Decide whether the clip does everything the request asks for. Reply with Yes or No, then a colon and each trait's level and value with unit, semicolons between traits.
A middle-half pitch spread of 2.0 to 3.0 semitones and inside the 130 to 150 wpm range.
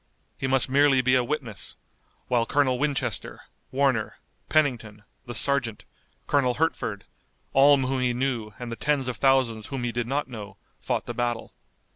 No: average, 2.7 semitones; average, 160 wpm